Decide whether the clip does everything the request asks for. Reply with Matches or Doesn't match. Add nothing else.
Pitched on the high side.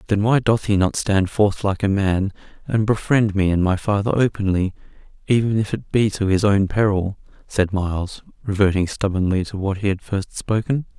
Doesn't match